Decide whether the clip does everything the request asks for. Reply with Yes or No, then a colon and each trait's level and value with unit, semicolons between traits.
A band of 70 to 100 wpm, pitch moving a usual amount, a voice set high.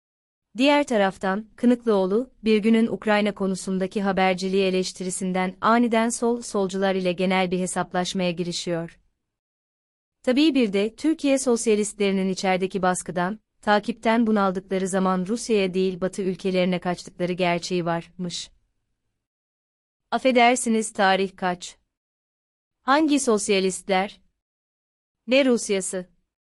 Yes: slow, 95 wpm; average, 3.3 semitones; high, 195 Hz